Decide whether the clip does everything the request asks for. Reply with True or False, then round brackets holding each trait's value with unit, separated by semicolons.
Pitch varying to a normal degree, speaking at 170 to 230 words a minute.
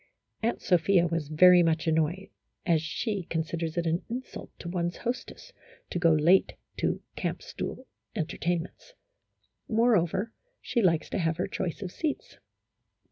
False (3.3 semitones; 145 wpm)